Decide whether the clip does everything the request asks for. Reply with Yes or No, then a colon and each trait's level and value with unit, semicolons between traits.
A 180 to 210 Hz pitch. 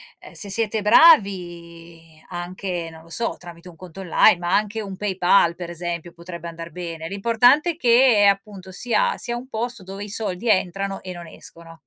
Yes: medium, 185 Hz